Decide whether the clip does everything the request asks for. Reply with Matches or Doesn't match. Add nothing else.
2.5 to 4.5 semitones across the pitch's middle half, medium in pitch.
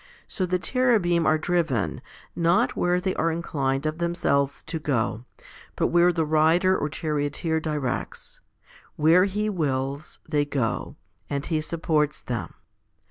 Matches